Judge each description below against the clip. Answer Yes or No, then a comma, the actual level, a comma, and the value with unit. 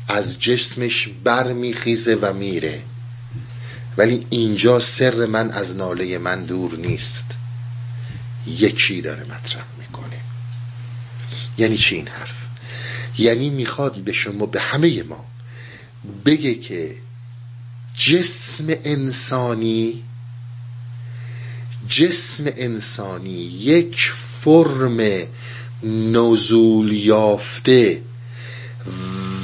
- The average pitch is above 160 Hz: No, low, 120 Hz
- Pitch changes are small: Yes, narrow, 1.1 semitones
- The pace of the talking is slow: Yes, slow, 80 wpm